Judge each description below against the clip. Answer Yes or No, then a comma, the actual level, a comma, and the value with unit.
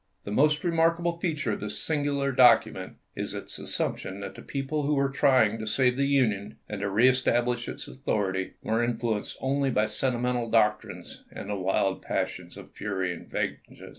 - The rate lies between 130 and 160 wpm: No, average, 175 wpm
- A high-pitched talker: No, low, 120 Hz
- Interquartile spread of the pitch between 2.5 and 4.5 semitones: No, average, 5.0 semitones